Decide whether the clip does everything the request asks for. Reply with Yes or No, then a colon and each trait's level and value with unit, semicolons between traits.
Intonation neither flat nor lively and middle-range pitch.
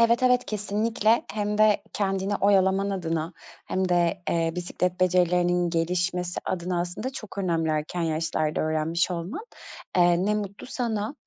Yes: average, 3.2 semitones; medium, 180 Hz